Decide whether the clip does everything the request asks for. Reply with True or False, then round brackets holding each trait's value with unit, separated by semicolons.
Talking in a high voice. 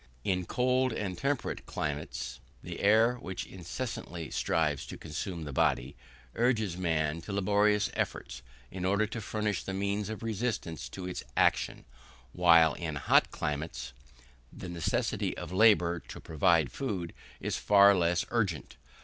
False (90 Hz)